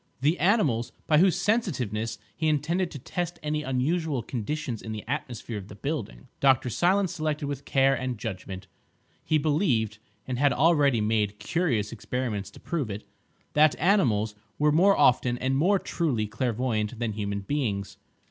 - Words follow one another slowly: No, average, 155 wpm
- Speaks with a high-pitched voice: No, low, 130 Hz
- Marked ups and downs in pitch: Yes, wide, 5.9 semitones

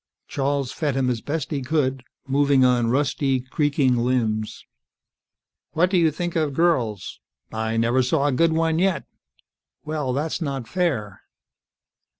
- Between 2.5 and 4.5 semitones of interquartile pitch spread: Yes, average, 3.9 semitones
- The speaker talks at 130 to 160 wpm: Yes, average, 145 wpm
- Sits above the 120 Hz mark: Yes, medium, 140 Hz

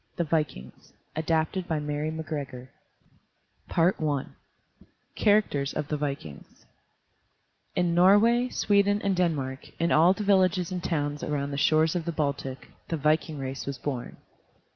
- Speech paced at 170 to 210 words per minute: No, slow, 135 wpm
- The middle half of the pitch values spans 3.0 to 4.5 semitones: Yes, average, 4.0 semitones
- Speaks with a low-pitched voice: No, medium, 155 Hz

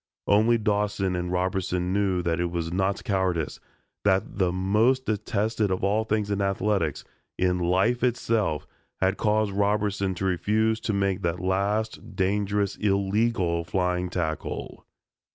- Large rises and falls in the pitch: No, narrow, 2.5 semitones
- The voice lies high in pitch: No, low, 100 Hz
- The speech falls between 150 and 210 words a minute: No, slow, 135 wpm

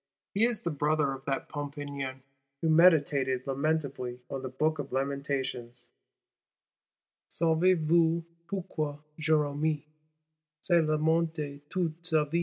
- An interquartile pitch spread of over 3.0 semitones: No, average, 2.7 semitones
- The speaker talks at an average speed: No, slow, 115 wpm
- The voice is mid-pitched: Yes, medium, 150 Hz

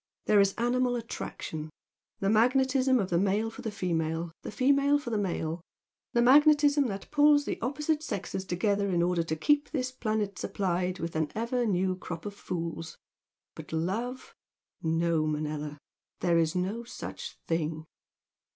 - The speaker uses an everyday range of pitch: No, wide, 6.9 semitones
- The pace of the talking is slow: No, average, 155 wpm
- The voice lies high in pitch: Yes, high, 200 Hz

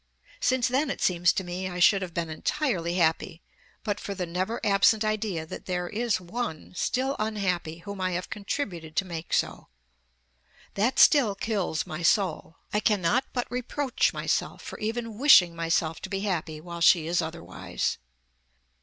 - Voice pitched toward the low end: No, high, 190 Hz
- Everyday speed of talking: Yes, average, 165 wpm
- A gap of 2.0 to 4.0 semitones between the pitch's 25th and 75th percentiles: No, average, 4.5 semitones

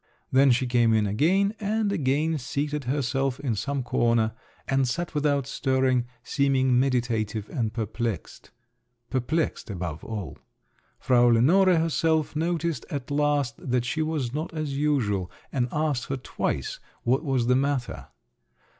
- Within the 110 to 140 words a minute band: Yes, slow, 135 wpm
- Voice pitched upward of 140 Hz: No, low, 135 Hz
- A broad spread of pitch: No, average, 3.8 semitones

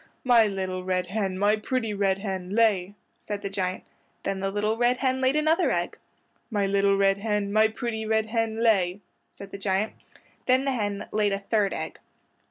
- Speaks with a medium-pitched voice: No, high, 205 Hz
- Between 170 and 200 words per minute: Yes, average, 185 wpm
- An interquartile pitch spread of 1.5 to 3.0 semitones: Yes, narrow, 2.4 semitones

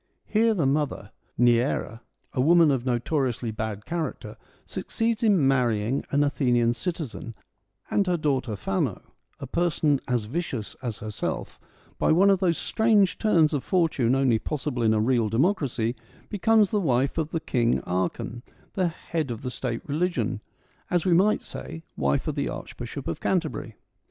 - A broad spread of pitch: Yes, wide, 6.5 semitones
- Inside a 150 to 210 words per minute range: Yes, average, 155 wpm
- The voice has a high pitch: No, medium, 140 Hz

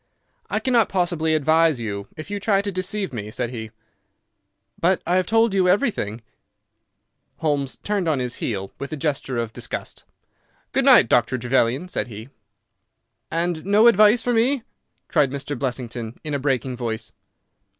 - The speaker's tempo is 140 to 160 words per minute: Yes, average, 155 wpm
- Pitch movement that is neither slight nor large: No, wide, 7.6 semitones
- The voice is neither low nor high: Yes, medium, 150 Hz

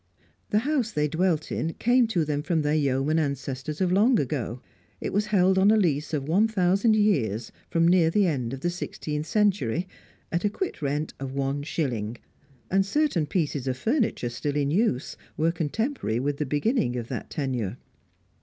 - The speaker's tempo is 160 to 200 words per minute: Yes, average, 180 wpm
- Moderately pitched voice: Yes, medium, 155 Hz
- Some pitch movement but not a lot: No, wide, 6.3 semitones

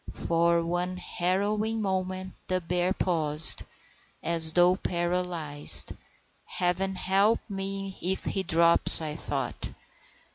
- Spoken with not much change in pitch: Yes, narrow, 2.1 semitones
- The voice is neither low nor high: Yes, medium, 180 Hz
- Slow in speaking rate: Yes, slow, 105 wpm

